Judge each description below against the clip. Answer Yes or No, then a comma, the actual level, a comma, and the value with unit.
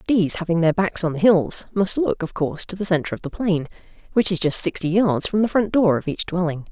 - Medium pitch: Yes, medium, 180 Hz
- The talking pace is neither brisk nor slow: No, fast, 260 wpm